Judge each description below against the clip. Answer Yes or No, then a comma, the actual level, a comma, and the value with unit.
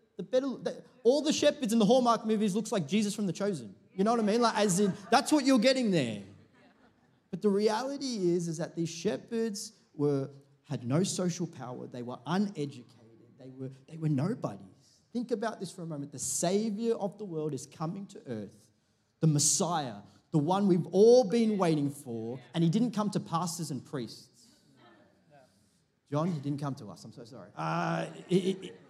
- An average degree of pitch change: No, wide, 7.3 semitones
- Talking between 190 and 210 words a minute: Yes, average, 195 wpm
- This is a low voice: No, medium, 180 Hz